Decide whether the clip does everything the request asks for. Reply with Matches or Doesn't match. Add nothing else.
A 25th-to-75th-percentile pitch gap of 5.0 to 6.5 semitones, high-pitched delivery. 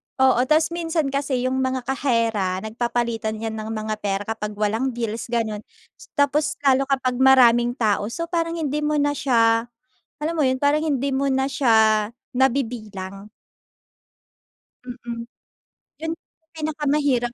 Doesn't match